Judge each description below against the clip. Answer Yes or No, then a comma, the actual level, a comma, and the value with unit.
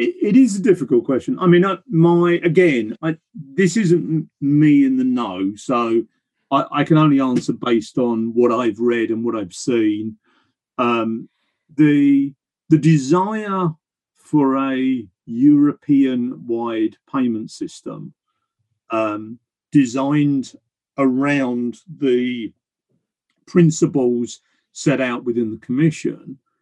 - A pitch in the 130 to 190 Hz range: Yes, low, 135 Hz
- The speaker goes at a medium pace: No, slow, 115 wpm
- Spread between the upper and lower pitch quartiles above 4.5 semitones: Yes, wide, 5.5 semitones